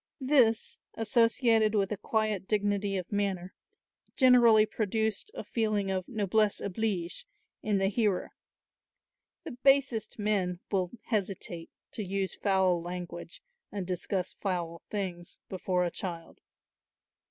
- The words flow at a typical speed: No, slow, 120 wpm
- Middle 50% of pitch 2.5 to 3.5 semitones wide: Yes, average, 3.1 semitones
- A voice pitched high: Yes, high, 200 Hz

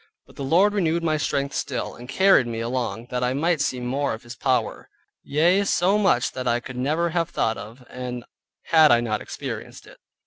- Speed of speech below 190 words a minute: No, average, 200 wpm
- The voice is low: Yes, low, 130 Hz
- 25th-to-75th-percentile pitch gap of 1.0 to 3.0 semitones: No, average, 5.2 semitones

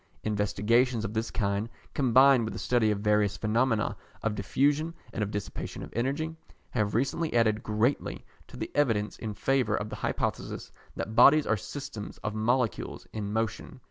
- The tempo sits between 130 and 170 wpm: Yes, average, 165 wpm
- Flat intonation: No, average, 3.7 semitones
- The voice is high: No, low, 110 Hz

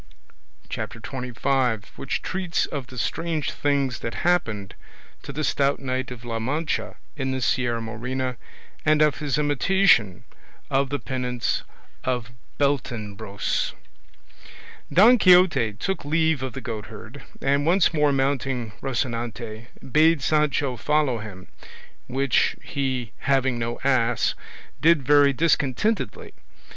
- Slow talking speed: Yes, slow, 120 wpm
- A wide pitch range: No, average, 3.8 semitones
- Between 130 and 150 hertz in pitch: Yes, low, 135 Hz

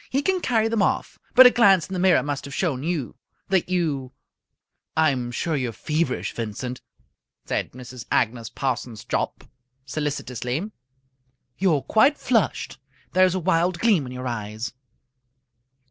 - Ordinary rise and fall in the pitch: No, wide, 6.9 semitones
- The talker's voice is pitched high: No, medium, 150 Hz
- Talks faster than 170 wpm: No, average, 155 wpm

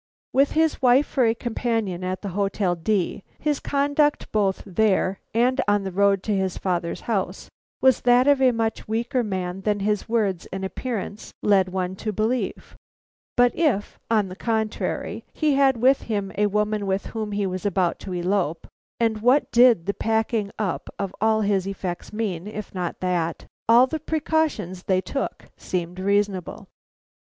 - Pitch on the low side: No, high, 210 Hz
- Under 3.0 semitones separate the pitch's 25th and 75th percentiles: No, average, 4.0 semitones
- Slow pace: No, average, 170 wpm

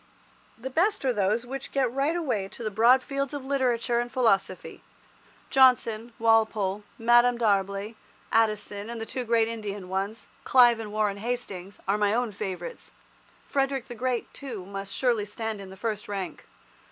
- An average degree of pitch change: Yes, average, 3.6 semitones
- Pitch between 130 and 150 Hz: No, high, 225 Hz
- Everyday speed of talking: Yes, average, 165 wpm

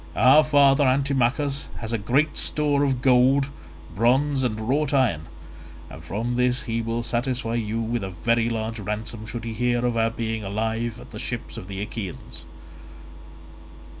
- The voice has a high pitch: No, low, 120 Hz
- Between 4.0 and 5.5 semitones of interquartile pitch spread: No, average, 3.0 semitones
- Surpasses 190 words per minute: No, average, 160 wpm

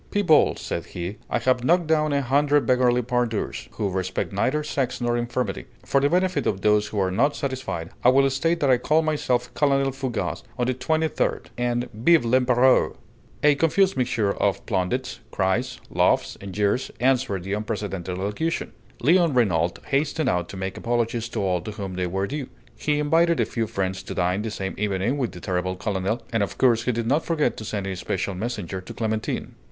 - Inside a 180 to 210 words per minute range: Yes, average, 195 wpm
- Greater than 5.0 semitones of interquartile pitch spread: Yes, wide, 5.6 semitones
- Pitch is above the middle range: No, low, 120 Hz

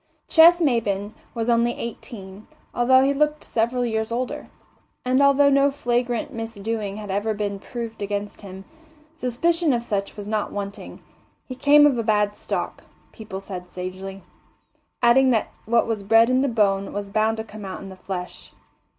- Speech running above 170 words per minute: No, average, 165 wpm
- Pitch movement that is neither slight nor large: Yes, average, 3.7 semitones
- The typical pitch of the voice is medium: No, high, 225 Hz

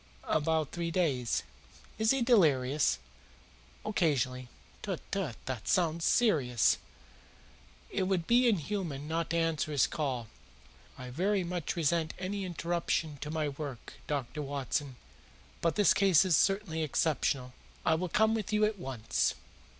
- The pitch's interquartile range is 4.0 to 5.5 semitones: Yes, average, 4.9 semitones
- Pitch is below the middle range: No, medium, 160 Hz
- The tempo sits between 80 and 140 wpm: Yes, slow, 135 wpm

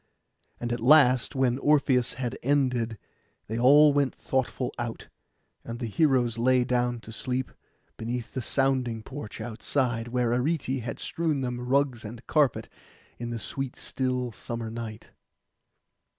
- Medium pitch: No, low, 125 Hz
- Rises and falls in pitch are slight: Yes, narrow, 2.2 semitones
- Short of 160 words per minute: Yes, average, 140 wpm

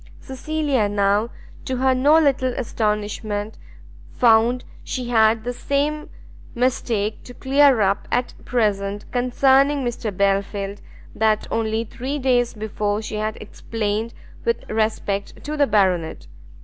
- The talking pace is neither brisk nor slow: No, slow, 125 wpm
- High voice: Yes, high, 225 Hz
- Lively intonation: No, average, 3.7 semitones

